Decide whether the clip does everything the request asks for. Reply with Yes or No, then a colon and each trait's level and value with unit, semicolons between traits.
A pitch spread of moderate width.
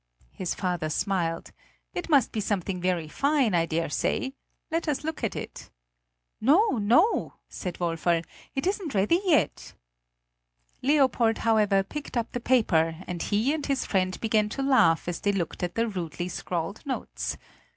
No: wide, 7.4 semitones